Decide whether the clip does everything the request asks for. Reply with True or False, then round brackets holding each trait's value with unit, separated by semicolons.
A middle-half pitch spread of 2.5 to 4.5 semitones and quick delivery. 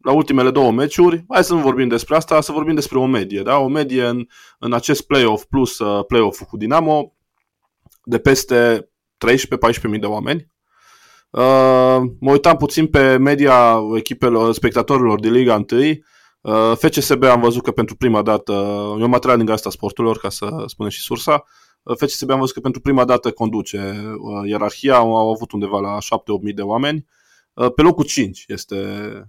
True (4.2 semitones; 180 wpm)